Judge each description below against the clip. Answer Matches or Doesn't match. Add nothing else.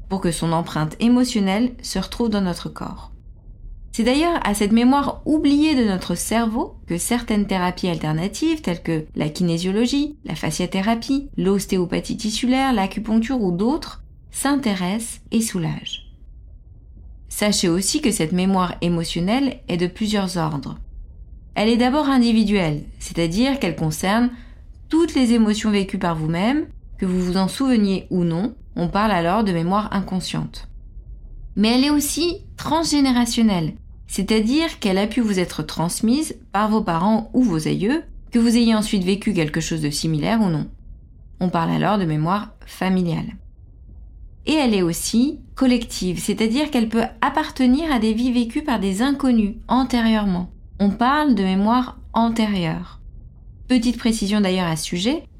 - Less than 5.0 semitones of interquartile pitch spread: Doesn't match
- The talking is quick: Doesn't match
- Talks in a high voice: Matches